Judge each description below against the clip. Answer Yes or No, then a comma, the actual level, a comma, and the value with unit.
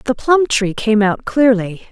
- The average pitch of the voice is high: Yes, high, 230 Hz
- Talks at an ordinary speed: Yes, average, 190 wpm